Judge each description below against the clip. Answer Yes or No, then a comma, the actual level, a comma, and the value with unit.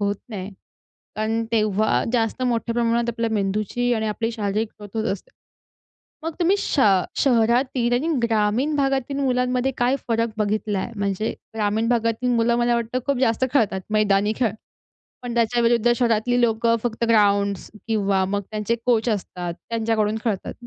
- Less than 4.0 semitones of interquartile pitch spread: Yes, narrow, 2.4 semitones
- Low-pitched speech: No, high, 230 Hz